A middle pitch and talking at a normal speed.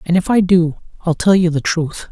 No: medium, 175 Hz; fast, 255 wpm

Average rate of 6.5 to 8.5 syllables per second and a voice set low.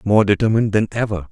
Yes: 6.8 syllables/s; low, 105 Hz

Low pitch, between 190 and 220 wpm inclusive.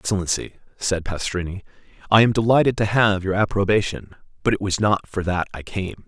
No: low, 100 Hz; average, 180 wpm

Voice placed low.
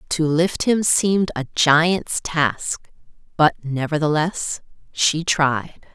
No: medium, 155 Hz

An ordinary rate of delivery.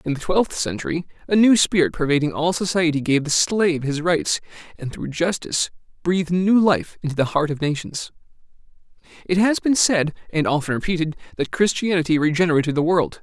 Yes: average, 170 wpm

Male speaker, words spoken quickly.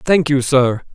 No: male; average, 190 wpm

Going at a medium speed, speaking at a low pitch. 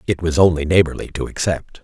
Yes: average, 195 wpm; very low, 85 Hz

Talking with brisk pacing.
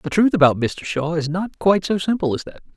Yes: fast, 260 wpm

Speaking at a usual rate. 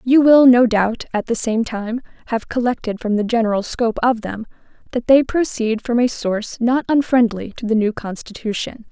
Yes: average, 190 wpm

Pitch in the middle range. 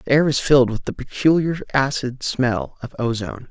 No: low, 130 Hz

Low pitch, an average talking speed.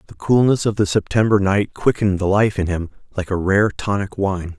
No: low, 100 Hz; fast, 210 wpm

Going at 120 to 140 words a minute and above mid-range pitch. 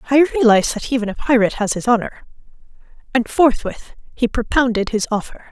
No: average, 165 wpm; high, 240 Hz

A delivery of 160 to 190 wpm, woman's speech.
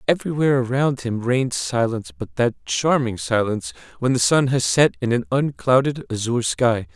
No: average, 165 wpm; male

